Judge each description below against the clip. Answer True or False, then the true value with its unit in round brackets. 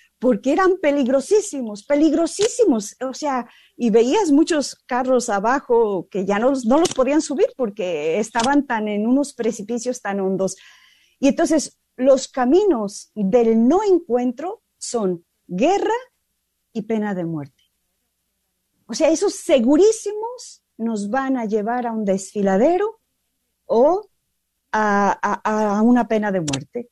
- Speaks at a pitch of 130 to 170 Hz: False (255 Hz)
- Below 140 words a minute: True (130 wpm)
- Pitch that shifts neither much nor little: False (7.0 semitones)